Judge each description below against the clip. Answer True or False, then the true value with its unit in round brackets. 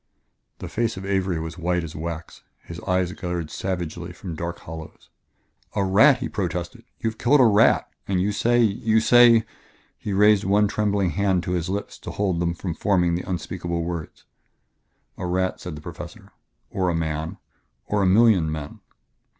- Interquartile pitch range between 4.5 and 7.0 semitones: False (3.2 semitones)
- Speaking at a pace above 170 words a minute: True (180 wpm)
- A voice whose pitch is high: False (90 Hz)